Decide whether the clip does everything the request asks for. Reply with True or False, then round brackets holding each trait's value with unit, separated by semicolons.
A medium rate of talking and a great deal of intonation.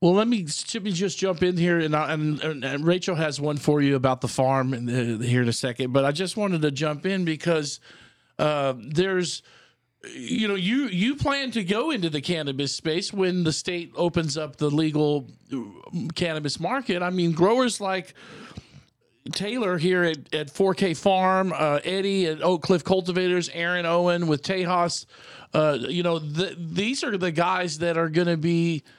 False (185 wpm; 3.8 semitones)